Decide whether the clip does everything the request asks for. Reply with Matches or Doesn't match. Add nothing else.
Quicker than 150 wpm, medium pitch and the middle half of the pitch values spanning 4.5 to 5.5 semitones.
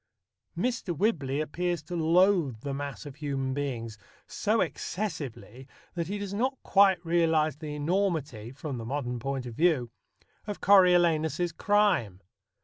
Doesn't match